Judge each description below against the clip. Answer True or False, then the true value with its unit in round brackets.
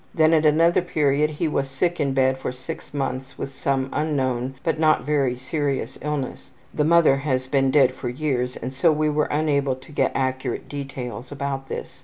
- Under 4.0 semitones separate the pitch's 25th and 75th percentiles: True (2.6 semitones)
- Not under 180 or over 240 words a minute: True (190 wpm)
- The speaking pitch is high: False (140 Hz)